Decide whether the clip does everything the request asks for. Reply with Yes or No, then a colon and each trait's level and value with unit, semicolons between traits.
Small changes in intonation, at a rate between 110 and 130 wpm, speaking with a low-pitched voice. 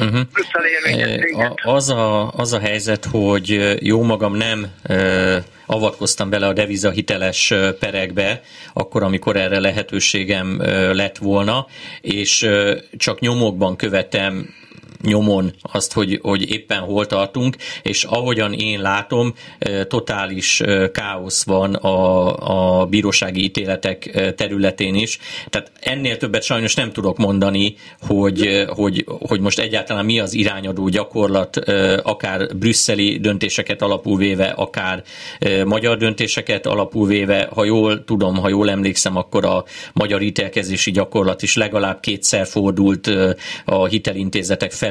Yes: narrow, 2.0 semitones; average, 120 wpm; low, 100 Hz